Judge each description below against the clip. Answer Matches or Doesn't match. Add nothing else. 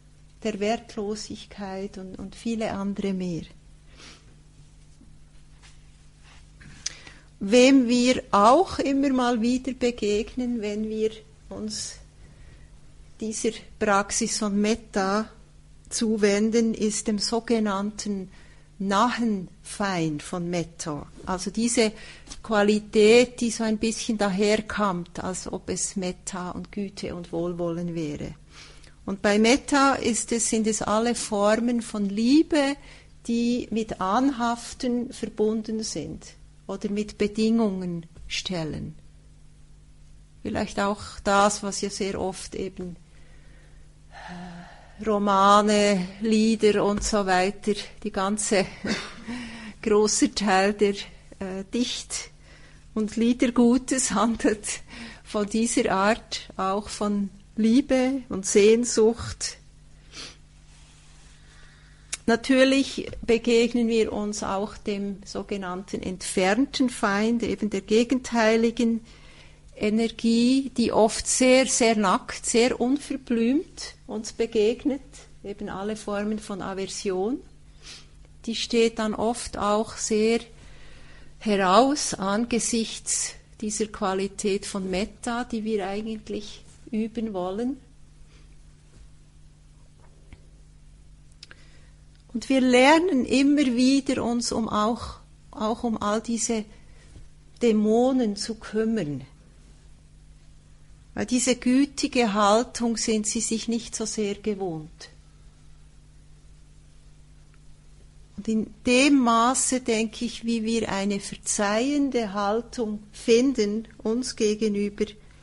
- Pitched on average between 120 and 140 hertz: Doesn't match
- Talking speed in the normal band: Doesn't match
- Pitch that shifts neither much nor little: Matches